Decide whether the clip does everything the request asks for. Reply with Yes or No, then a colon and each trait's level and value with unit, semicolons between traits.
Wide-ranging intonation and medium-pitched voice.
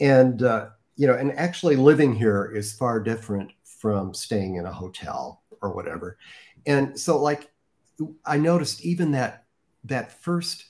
No: wide, 6.1 semitones; low, 130 Hz